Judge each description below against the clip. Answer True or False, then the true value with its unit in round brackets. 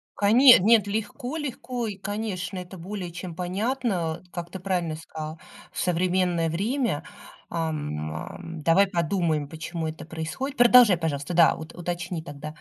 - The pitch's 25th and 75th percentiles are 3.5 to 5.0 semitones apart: True (4.1 semitones)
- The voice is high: False (175 Hz)